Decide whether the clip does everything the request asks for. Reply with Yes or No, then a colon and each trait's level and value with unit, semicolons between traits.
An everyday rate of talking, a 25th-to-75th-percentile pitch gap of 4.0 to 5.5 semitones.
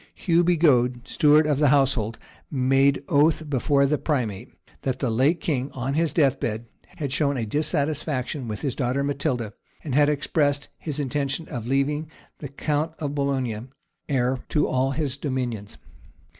No: average, 155 wpm; average, 2.8 semitones